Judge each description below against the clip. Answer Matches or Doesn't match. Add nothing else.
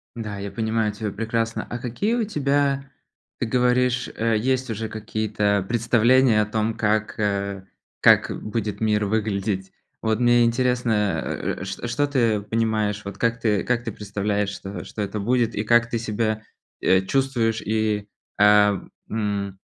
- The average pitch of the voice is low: Matches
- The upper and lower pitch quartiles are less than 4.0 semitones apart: Matches